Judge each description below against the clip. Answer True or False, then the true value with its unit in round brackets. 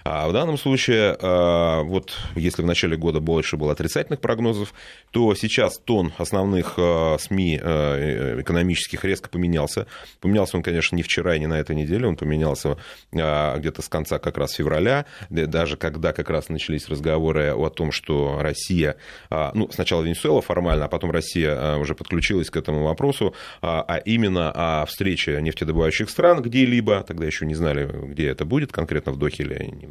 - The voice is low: True (85 Hz)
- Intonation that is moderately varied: True (3.7 semitones)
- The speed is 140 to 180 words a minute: True (160 wpm)